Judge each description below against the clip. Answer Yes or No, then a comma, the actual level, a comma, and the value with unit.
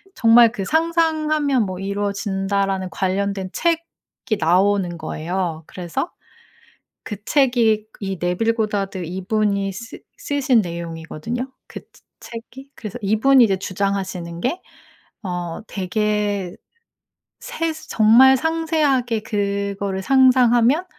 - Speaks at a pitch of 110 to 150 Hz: No, high, 205 Hz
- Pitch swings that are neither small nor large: Yes, average, 5.0 semitones